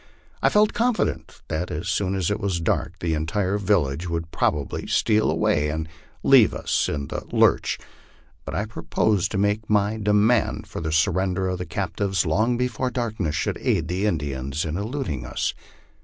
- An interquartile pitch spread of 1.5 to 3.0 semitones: No, average, 4.8 semitones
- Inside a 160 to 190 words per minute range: Yes, average, 170 wpm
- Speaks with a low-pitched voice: Yes, very low, 95 Hz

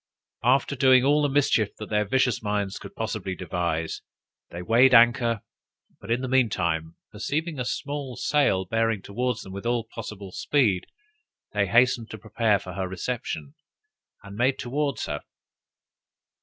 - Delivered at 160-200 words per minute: No, average, 150 wpm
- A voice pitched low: Yes, low, 115 Hz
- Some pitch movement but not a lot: Yes, average, 4.5 semitones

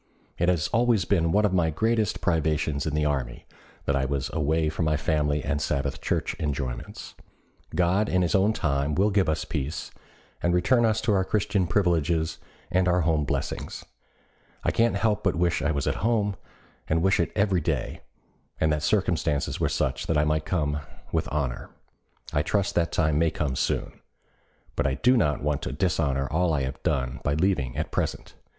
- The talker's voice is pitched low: Yes, very low, 80 Hz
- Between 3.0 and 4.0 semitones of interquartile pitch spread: No, average, 4.5 semitones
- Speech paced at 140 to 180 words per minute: No, average, 190 wpm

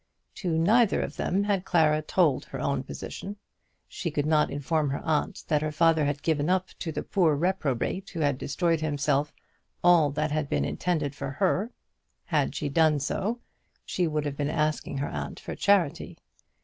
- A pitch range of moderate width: Yes, average, 3.5 semitones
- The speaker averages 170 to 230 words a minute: Yes, average, 180 wpm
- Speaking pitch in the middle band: Yes, medium, 155 Hz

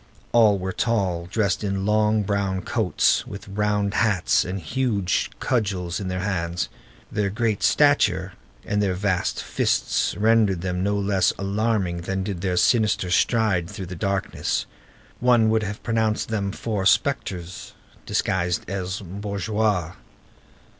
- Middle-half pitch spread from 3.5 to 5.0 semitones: No, average, 2.7 semitones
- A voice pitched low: Yes, low, 100 Hz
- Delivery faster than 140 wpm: No, slow, 135 wpm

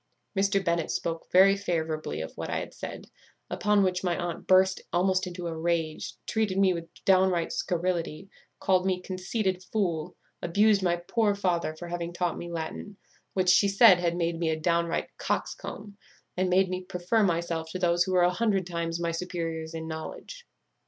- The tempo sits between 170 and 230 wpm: Yes, average, 180 wpm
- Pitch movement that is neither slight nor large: No, narrow, 2.0 semitones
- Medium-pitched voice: Yes, medium, 180 Hz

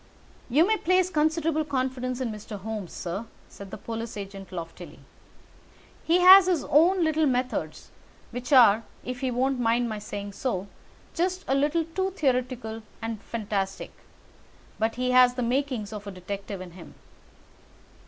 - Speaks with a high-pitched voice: Yes, high, 245 Hz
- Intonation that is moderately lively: No, wide, 6.3 semitones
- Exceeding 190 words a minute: No, average, 155 wpm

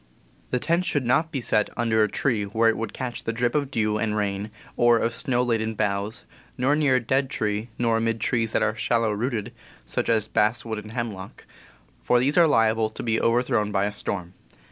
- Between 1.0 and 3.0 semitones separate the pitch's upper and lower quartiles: Yes, narrow, 2.4 semitones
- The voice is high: No, low, 115 Hz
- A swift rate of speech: Yes, fast, 210 wpm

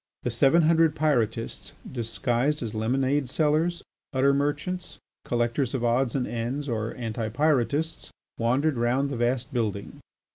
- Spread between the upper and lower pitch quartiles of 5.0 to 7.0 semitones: No, average, 3.8 semitones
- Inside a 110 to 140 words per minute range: Yes, slow, 135 wpm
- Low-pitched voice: Yes, low, 130 Hz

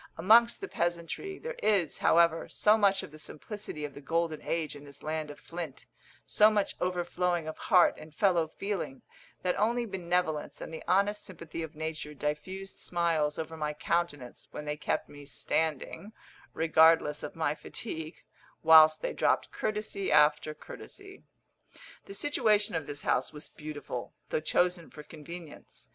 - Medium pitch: Yes, medium, 165 Hz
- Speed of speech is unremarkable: Yes, average, 155 wpm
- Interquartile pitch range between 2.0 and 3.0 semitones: No, average, 4.1 semitones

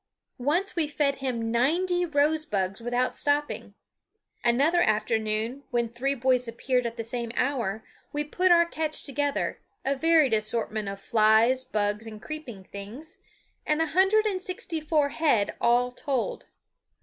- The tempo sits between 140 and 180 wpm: Yes, average, 145 wpm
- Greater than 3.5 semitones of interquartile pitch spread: Yes, average, 5.2 semitones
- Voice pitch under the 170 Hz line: No, very high, 260 Hz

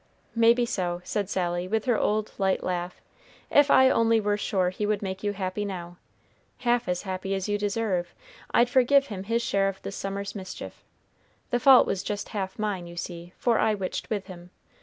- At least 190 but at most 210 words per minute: Yes, average, 195 wpm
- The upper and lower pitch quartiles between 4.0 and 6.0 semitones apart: No, average, 3.2 semitones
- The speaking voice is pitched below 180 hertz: No, high, 200 Hz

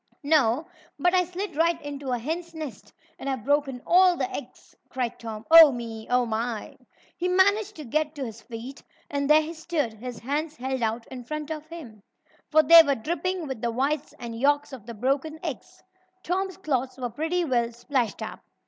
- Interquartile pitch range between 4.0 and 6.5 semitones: Yes, average, 5.2 semitones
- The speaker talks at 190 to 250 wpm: Yes, average, 195 wpm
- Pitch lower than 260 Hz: No, very high, 285 Hz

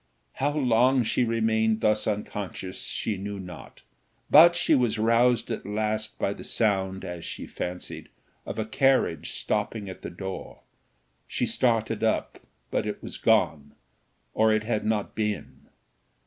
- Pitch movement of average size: No, narrow, 2.3 semitones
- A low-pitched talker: Yes, low, 110 Hz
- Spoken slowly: No, average, 150 wpm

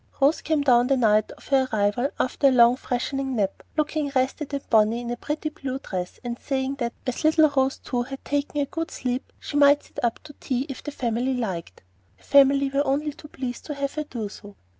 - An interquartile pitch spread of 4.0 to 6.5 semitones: No, average, 3.0 semitones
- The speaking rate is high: Yes, fast, 225 wpm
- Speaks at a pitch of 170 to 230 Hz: No, very high, 265 Hz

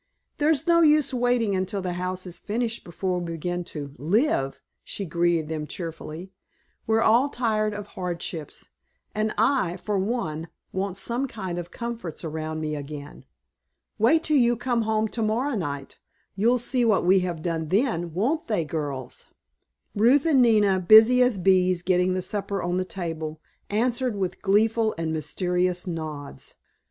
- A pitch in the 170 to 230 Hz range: Yes, high, 190 Hz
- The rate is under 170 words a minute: Yes, average, 160 wpm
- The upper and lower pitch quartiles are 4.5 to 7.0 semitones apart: Yes, average, 5.3 semitones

